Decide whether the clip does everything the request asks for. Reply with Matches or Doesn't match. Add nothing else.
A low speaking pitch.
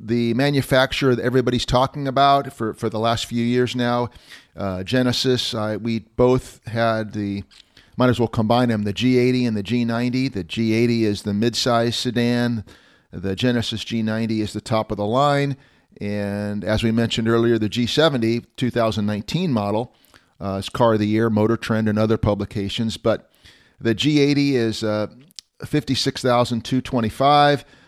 Matches